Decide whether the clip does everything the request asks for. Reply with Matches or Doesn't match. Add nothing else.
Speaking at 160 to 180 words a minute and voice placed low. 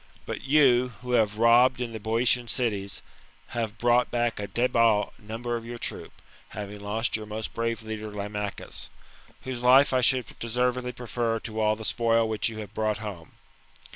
Matches